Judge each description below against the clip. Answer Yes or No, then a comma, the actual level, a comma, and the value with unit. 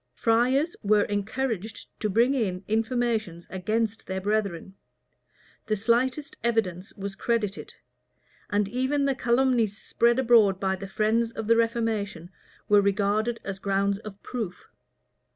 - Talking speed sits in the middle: No, slow, 130 wpm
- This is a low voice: No, high, 215 Hz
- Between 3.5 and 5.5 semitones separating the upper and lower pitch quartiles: No, average, 3.0 semitones